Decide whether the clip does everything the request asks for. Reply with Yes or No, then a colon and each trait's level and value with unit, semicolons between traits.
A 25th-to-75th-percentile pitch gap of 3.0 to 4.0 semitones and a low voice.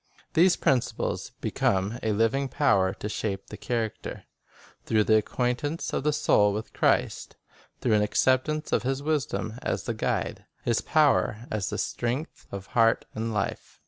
No: average, 4.5 semitones; low, 115 Hz